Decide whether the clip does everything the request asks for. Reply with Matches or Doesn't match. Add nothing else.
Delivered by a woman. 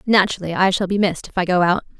Matches